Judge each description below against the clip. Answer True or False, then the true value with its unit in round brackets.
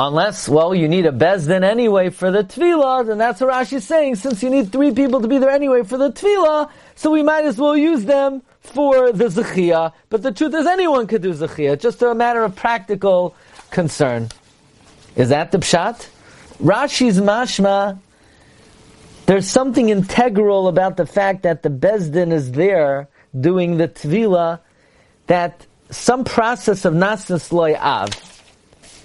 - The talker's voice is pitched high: True (205 Hz)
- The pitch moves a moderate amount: False (7.1 semitones)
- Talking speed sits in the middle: True (165 wpm)